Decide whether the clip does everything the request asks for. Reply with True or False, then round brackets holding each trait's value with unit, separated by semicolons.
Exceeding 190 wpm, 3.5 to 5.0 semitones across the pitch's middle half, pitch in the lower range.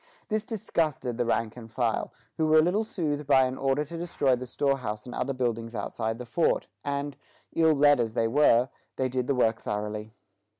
True (200 wpm; 4.4 semitones; 130 Hz)